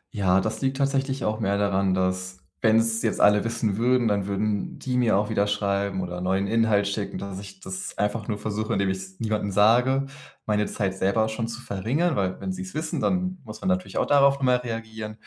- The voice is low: Yes, low, 110 Hz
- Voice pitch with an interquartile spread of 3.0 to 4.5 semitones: Yes, average, 3.6 semitones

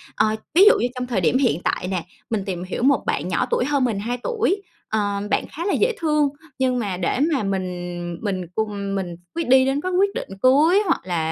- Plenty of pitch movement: Yes, wide, 7.4 semitones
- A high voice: Yes, high, 235 Hz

